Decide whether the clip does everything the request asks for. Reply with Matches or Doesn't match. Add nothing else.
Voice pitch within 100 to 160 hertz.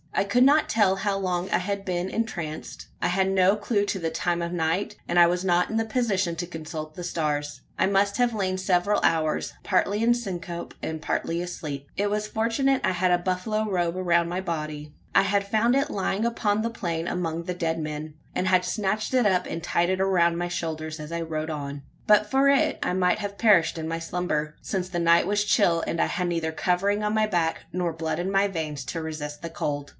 Doesn't match